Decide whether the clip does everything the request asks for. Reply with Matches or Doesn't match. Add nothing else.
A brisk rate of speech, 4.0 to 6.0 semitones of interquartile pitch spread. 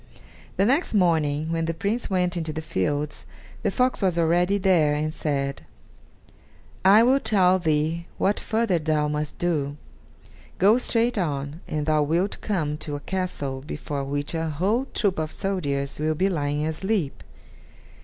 Doesn't match